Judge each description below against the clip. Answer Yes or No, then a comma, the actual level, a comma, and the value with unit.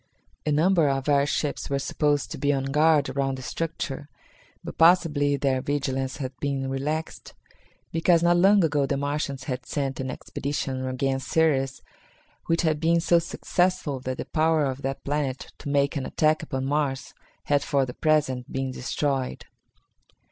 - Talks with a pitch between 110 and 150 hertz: Yes, medium, 140 Hz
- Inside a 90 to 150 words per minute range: No, average, 165 wpm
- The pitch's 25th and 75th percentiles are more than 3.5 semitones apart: No, narrow, 2.6 semitones